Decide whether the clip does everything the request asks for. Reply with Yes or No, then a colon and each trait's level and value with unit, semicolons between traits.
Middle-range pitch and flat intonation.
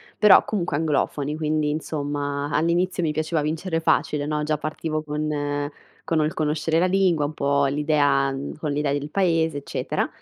Yes: medium, 150 Hz; narrow, 1.9 semitones